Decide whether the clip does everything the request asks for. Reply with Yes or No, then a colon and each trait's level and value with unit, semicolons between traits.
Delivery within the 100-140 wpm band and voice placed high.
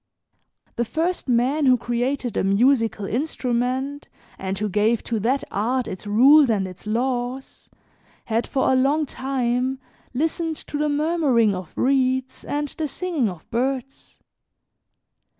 Yes: slow, 135 wpm; very high, 255 Hz